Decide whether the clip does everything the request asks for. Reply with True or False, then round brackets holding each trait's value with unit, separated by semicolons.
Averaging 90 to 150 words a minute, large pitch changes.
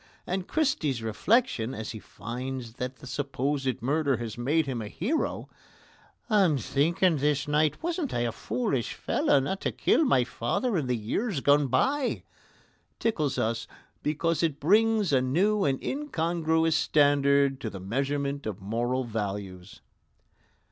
True (145 wpm; 5.9 semitones)